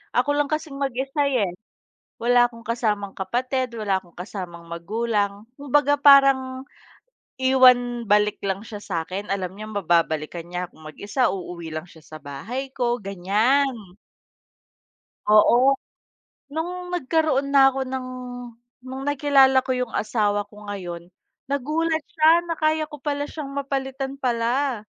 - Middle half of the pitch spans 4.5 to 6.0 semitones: Yes, wide, 5.6 semitones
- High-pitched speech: Yes, high, 245 Hz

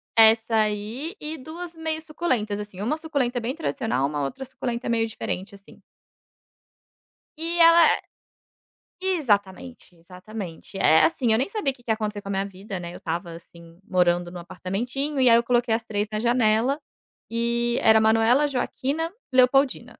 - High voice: Yes, high, 230 Hz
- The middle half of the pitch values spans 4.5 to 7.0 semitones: Yes, average, 5.2 semitones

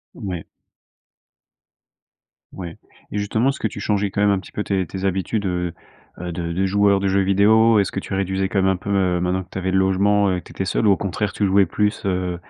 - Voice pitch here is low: Yes, very low, 95 Hz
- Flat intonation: Yes, narrow, 1.7 semitones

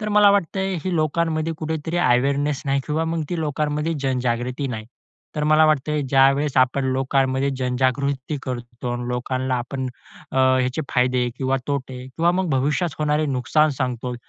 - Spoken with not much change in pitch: No, average, 3.3 semitones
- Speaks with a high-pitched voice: No, low, 135 Hz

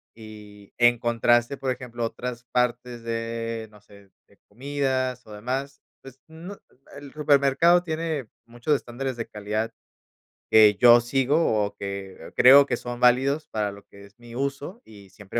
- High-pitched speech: No, low, 120 Hz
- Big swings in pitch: No, average, 3.8 semitones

